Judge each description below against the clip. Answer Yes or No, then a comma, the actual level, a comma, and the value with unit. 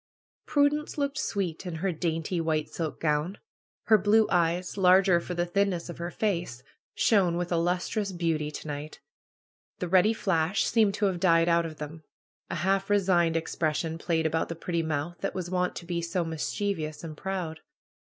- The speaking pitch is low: No, medium, 175 Hz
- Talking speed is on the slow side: No, average, 180 wpm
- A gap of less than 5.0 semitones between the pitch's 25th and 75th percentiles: Yes, average, 3.0 semitones